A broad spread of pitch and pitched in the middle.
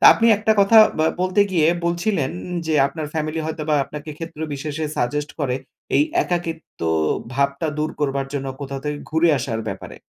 No: average, 3.1 semitones; medium, 155 Hz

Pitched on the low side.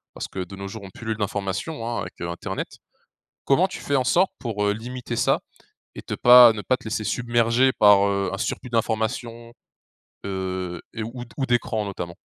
Yes: low, 110 Hz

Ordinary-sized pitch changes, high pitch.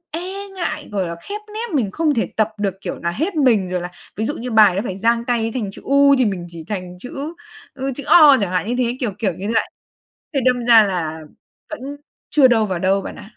No: wide, 6.4 semitones; high, 225 Hz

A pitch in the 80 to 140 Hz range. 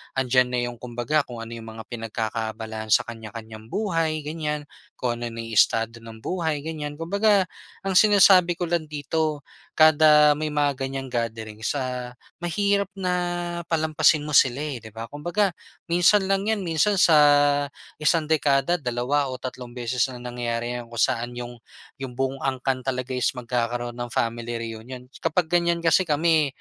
Yes: low, 135 Hz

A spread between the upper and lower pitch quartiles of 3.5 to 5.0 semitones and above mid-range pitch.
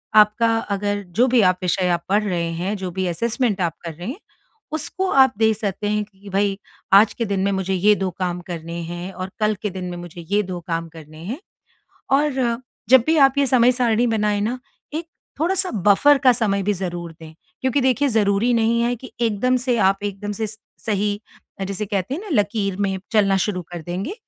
Yes: average, 3.9 semitones; high, 205 Hz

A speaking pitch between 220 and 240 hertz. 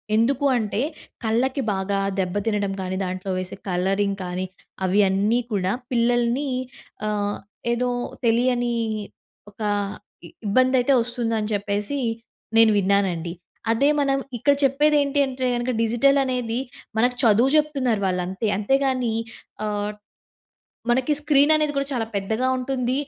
Yes: high, 230 Hz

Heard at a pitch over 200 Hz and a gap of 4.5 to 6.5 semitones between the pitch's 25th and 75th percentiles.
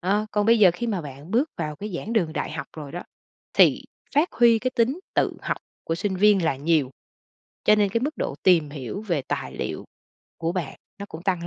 No: high, 190 Hz; average, 5.2 semitones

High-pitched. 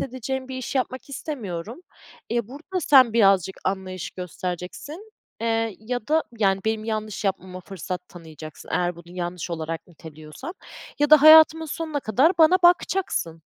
Yes: high, 220 Hz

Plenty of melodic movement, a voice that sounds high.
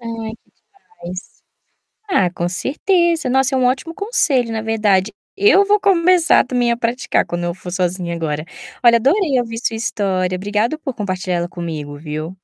Yes: wide, 6.8 semitones; high, 225 Hz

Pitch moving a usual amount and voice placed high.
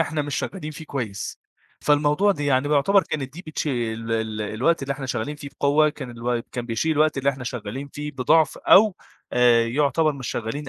No: average, 3.7 semitones; medium, 140 Hz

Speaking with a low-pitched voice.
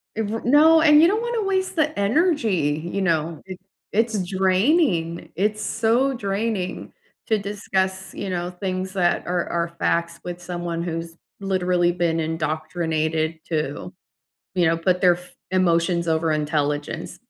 No: medium, 180 Hz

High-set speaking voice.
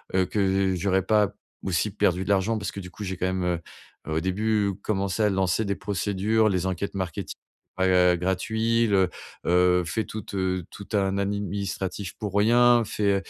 No: low, 100 Hz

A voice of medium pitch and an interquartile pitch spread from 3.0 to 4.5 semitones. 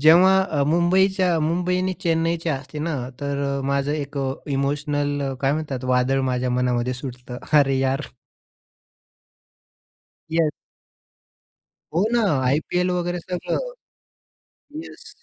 Yes: medium, 145 Hz; average, 4.2 semitones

